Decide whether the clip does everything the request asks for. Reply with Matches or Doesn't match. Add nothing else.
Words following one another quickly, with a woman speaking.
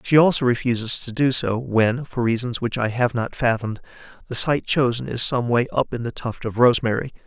Doesn't match